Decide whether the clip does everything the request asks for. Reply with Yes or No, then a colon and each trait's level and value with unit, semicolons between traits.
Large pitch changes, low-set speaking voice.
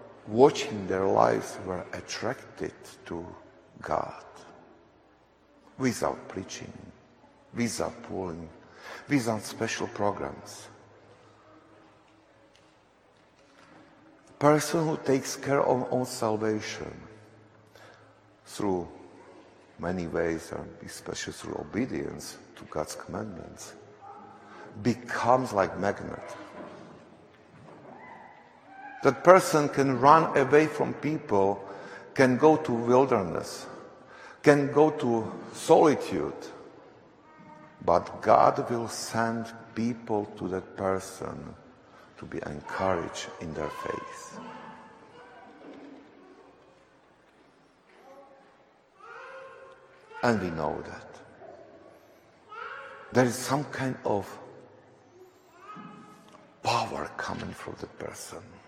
Yes: wide, 6.2 semitones; low, 125 Hz